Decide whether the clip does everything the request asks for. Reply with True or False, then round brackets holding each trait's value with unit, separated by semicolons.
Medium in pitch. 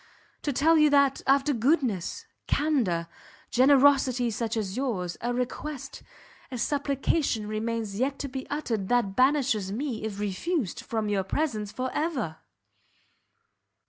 False (250 Hz)